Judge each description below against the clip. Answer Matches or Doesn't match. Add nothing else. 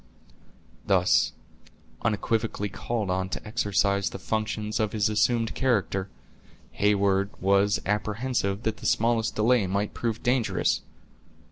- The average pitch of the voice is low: Matches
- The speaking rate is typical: Doesn't match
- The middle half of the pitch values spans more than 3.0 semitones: Doesn't match